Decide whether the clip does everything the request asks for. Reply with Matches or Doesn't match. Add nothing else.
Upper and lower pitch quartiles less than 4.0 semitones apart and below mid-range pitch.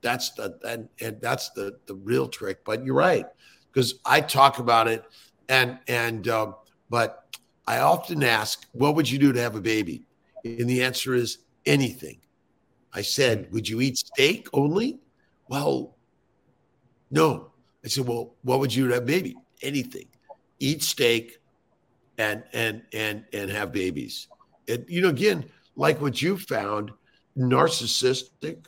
Matches